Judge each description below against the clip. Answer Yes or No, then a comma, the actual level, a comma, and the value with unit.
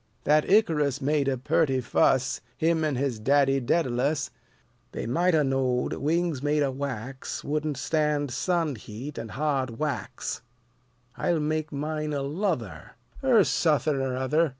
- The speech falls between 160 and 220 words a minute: No, average, 145 wpm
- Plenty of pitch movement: No, average, 2.9 semitones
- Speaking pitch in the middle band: Yes, medium, 145 Hz